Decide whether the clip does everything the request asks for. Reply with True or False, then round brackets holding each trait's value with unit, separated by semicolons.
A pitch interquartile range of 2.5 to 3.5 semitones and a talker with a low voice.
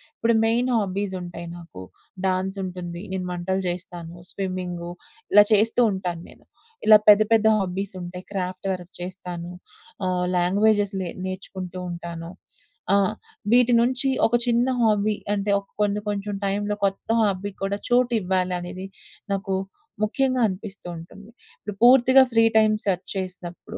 False (2.8 semitones; 190 Hz)